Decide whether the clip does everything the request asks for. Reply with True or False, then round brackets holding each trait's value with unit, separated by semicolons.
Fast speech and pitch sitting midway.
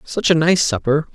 True (210 wpm; 155 Hz)